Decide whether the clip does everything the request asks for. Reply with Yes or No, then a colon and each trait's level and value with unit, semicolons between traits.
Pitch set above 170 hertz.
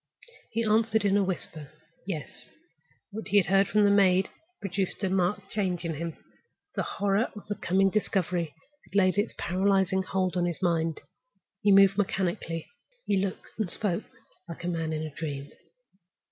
Yes: high, 190 Hz